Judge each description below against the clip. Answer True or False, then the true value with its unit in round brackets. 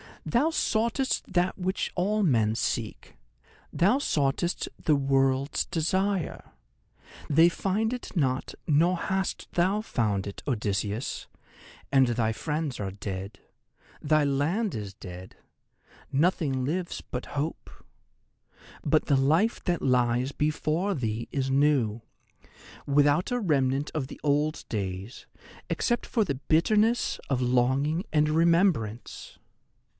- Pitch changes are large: True (6.4 semitones)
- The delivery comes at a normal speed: False (115 wpm)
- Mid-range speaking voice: True (145 Hz)